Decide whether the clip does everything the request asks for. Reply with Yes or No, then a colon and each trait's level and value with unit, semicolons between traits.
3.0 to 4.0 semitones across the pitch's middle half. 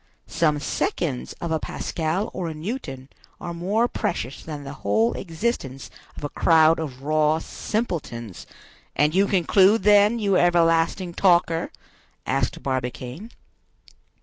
No: wide, 5.4 semitones